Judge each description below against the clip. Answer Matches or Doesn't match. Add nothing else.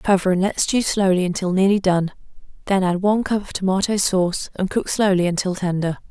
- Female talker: Matches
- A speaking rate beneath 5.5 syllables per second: Doesn't match